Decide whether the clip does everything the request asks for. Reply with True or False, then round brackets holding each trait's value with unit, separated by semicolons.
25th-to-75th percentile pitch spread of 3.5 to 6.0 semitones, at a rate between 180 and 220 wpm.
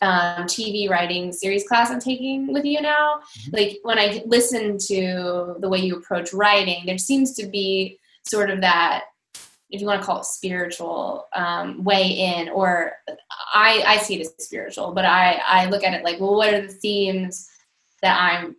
False (2.9 semitones; 185 wpm)